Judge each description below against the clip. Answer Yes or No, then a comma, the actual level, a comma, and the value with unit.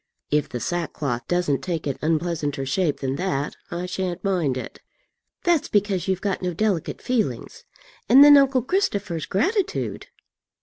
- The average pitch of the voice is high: No, medium, 180 Hz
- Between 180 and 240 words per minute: No, average, 145 wpm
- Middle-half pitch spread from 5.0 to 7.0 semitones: Yes, wide, 5.5 semitones